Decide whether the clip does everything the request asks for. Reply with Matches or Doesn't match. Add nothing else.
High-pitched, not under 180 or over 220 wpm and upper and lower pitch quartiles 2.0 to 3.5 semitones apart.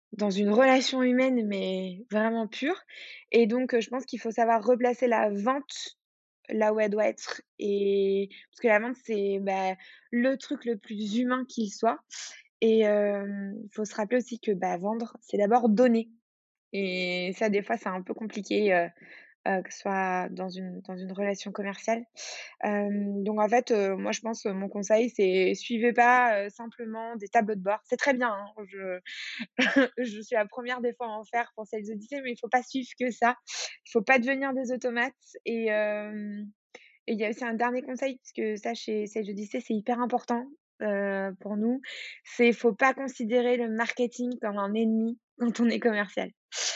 Matches